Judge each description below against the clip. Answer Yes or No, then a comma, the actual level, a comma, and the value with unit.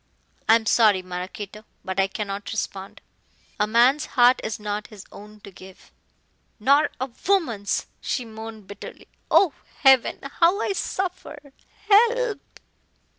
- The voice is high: Yes, high, 220 Hz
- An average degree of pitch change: No, wide, 5.7 semitones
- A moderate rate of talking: No, slow, 130 wpm